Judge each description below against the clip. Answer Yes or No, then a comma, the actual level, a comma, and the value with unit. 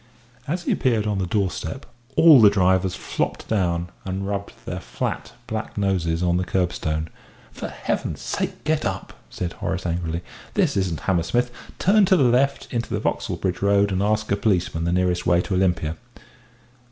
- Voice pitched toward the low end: Yes, very low, 95 Hz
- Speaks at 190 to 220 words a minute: No, average, 175 wpm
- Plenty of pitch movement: No, average, 3.6 semitones